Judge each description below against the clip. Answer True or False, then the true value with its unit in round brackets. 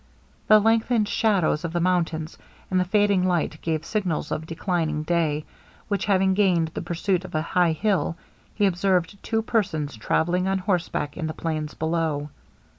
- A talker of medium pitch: True (175 Hz)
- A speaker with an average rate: True (165 wpm)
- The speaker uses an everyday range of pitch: True (3.5 semitones)